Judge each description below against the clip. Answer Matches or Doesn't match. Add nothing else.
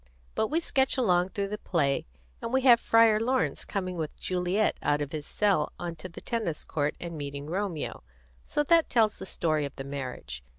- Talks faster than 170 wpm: Matches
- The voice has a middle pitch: Matches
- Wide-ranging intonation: Matches